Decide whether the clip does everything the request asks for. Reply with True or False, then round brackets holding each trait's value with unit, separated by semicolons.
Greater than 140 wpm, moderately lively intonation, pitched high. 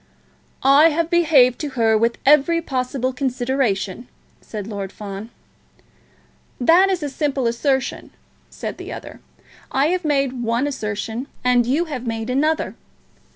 False (135 wpm; 4.2 semitones; 260 Hz)